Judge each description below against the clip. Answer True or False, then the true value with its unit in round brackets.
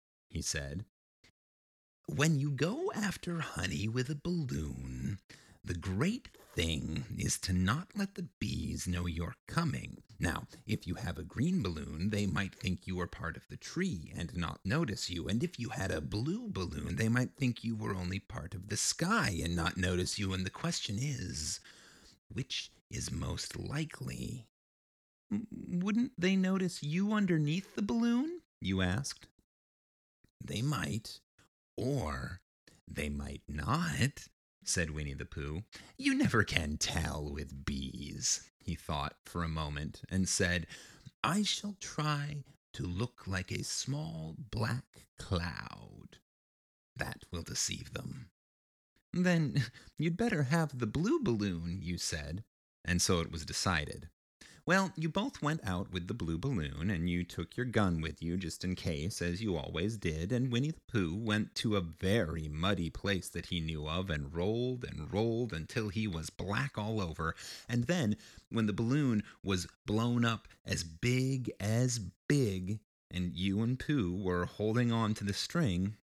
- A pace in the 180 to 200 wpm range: False (160 wpm)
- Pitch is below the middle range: True (100 Hz)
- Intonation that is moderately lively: False (7.5 semitones)